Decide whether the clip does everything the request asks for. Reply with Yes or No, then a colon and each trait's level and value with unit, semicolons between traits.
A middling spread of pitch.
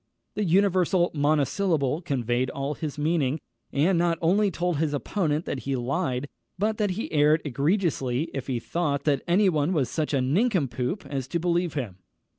Yes: average, 4.4 semitones